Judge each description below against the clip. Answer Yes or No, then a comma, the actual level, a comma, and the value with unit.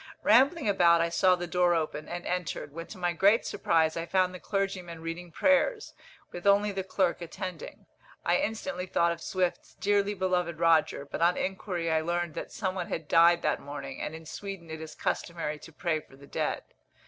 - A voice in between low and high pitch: Yes, medium, 175 Hz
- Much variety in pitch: No, narrow, 2.5 semitones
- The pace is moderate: Yes, average, 195 wpm